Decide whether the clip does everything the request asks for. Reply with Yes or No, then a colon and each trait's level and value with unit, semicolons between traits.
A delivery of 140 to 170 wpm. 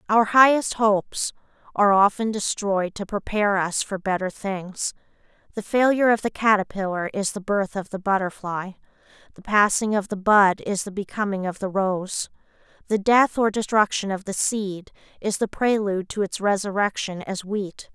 Yes: average, 165 wpm